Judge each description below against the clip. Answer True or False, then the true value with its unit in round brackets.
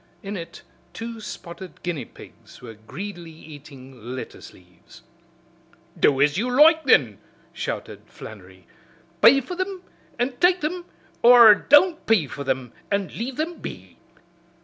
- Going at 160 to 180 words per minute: False (135 wpm)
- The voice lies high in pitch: True (195 Hz)